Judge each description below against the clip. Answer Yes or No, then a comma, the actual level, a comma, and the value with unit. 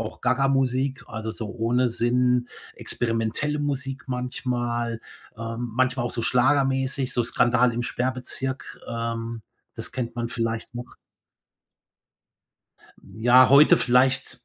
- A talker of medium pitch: No, low, 125 Hz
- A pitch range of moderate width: No, narrow, 1.9 semitones